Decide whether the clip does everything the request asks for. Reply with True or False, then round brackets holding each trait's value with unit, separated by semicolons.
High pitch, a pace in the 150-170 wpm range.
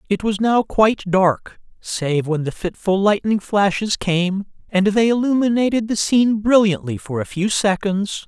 True (200 Hz; 160 wpm)